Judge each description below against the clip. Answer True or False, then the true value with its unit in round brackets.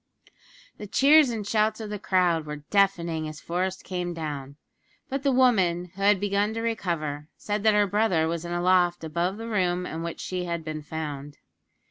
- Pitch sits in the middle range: True (180 Hz)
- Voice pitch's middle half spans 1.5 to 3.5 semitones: False (4.2 semitones)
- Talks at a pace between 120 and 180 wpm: False (190 wpm)